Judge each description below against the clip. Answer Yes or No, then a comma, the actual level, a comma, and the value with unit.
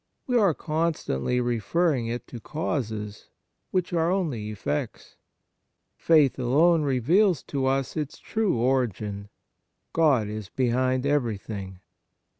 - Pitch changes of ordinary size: No, wide, 6.5 semitones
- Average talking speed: No, slow, 115 wpm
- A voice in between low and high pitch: No, low, 130 Hz